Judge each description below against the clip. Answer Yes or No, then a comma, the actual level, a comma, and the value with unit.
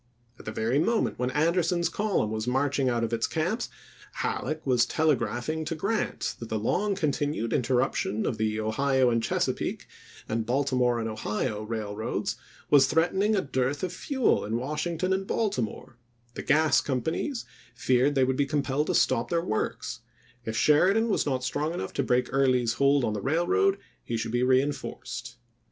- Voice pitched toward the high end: No, low, 135 Hz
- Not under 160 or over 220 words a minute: Yes, average, 170 wpm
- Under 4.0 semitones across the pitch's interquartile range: No, average, 5.3 semitones